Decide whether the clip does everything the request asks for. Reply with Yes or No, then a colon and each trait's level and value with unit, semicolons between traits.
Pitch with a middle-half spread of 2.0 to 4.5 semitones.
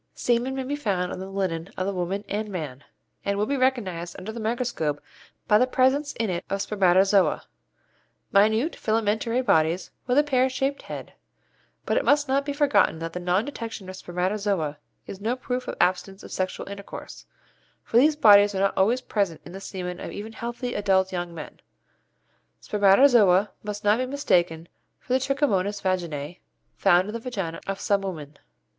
No: average, 5.1 semitones